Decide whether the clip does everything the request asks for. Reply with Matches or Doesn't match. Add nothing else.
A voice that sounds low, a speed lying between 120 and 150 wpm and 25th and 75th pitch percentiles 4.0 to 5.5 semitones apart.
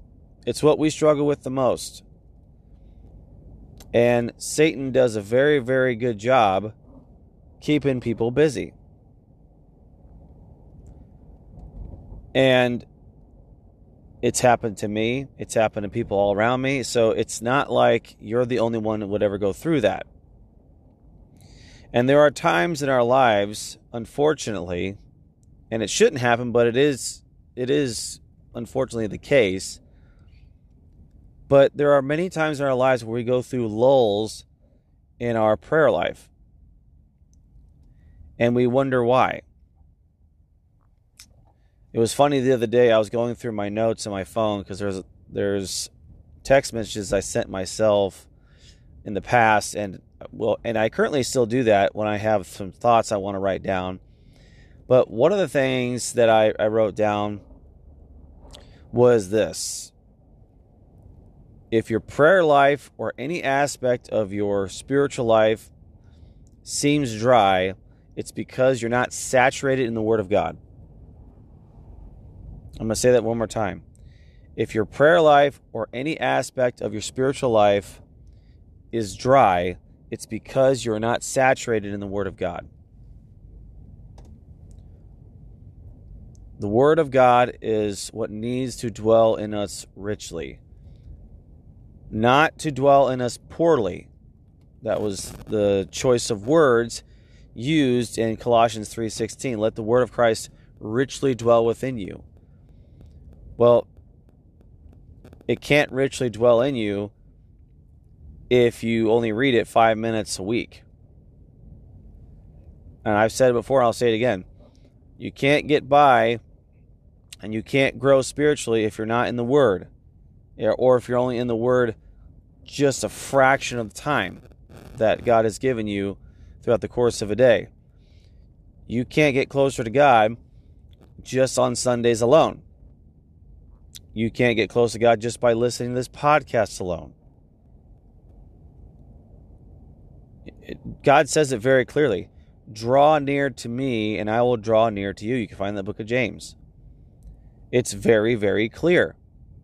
Matches